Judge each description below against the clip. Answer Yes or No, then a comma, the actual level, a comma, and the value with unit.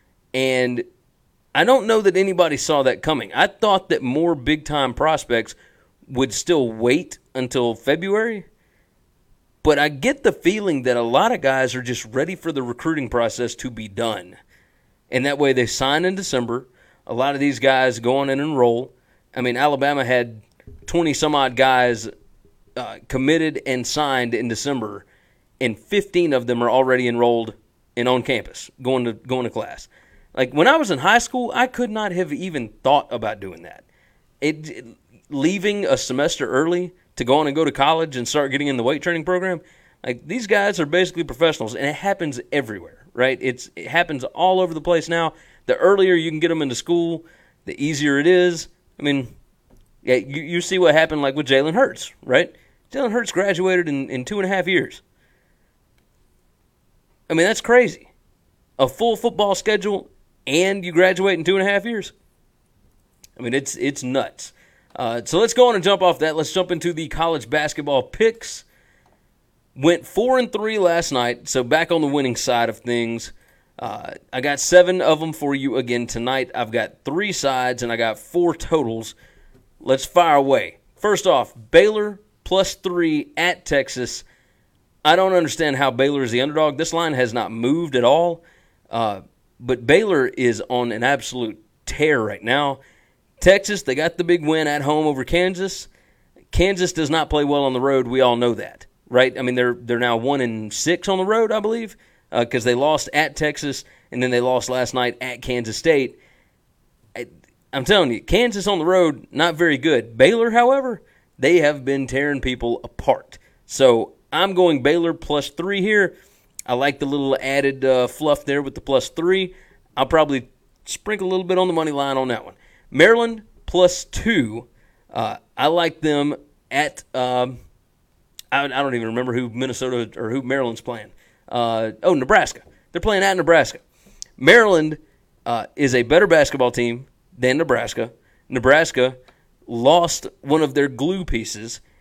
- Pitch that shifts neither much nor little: No, wide, 6.0 semitones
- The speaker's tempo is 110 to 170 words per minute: No, average, 180 wpm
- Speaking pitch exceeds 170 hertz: No, medium, 145 Hz